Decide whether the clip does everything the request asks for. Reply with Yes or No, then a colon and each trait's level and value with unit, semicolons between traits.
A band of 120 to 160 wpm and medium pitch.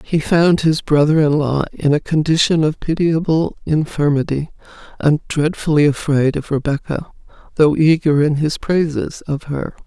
Yes: average, 140 wpm; medium, 150 Hz